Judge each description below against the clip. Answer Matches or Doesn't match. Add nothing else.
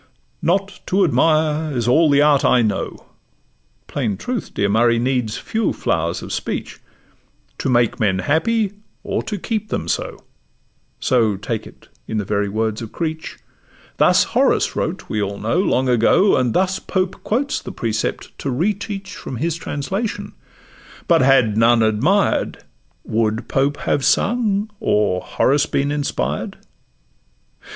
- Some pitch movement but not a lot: Doesn't match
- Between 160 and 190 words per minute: Doesn't match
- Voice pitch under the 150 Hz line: Matches